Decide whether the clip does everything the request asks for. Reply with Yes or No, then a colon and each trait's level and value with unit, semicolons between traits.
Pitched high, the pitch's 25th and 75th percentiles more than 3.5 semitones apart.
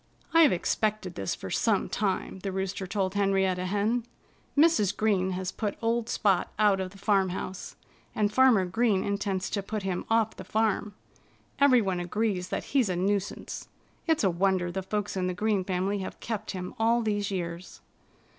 No: high, 200 Hz; narrow, 2.6 semitones